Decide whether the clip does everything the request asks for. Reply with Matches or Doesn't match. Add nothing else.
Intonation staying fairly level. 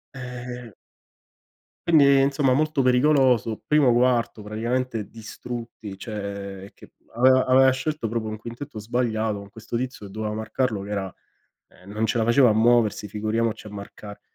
Doesn't match